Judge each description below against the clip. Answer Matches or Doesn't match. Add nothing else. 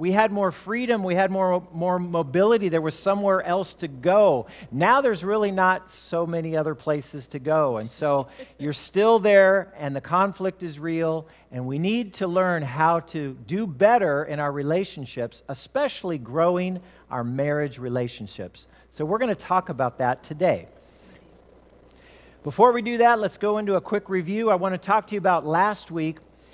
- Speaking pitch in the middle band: Matches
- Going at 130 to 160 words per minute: Doesn't match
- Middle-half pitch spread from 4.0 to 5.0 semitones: Matches